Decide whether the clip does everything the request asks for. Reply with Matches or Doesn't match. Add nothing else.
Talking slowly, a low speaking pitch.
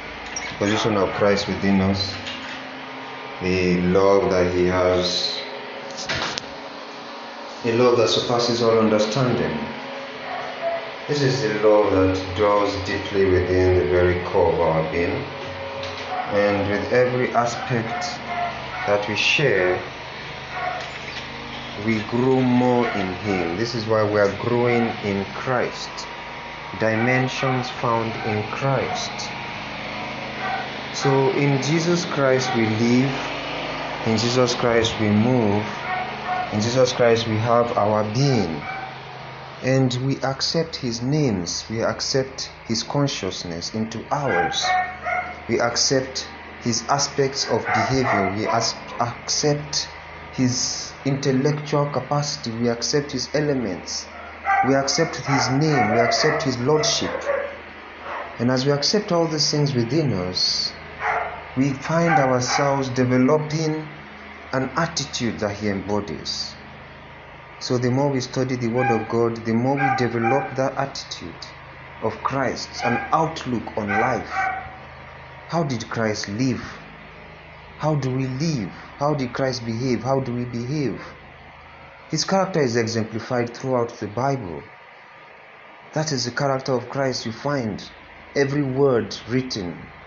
Matches